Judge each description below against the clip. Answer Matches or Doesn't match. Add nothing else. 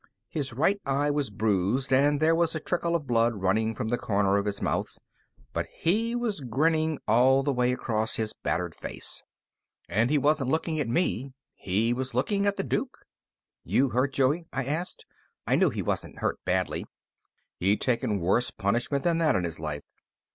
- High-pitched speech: Doesn't match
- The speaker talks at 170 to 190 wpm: Matches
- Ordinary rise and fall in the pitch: Doesn't match